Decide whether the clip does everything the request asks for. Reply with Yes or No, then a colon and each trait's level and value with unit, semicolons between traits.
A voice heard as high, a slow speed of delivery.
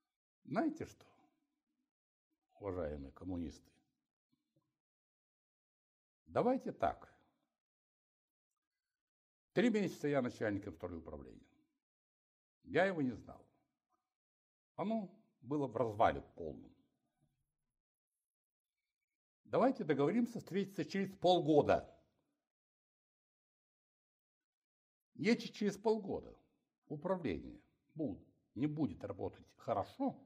Yes: high, 220 Hz; slow, 70 wpm